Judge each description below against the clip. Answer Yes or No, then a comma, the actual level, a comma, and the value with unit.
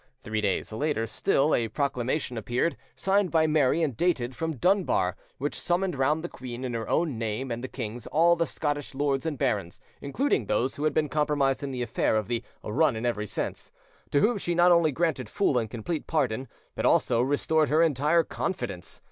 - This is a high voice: No, medium, 140 Hz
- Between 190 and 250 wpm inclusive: Yes, average, 200 wpm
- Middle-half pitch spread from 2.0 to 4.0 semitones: No, average, 5.1 semitones